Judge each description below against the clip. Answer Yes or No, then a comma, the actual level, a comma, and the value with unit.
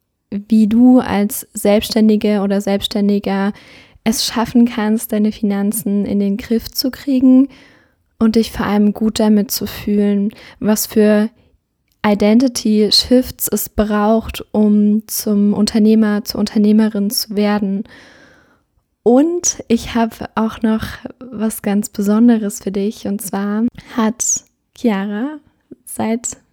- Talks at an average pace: No, slow, 120 wpm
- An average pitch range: No, narrow, 1.9 semitones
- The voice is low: No, high, 215 Hz